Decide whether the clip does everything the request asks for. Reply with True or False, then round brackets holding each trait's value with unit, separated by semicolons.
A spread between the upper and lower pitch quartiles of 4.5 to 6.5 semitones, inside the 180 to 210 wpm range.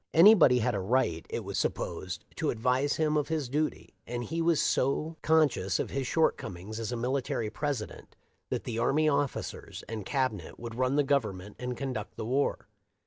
True (4.9 semitones; 185 wpm)